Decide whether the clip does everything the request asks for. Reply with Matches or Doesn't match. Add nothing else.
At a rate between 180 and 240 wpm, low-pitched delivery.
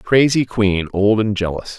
Matches